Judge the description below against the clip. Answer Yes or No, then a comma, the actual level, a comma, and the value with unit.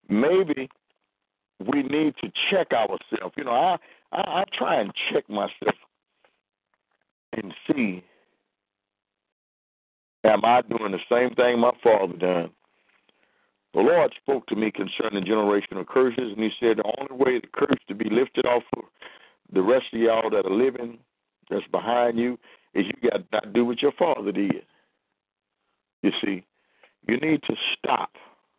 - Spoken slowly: No, average, 155 wpm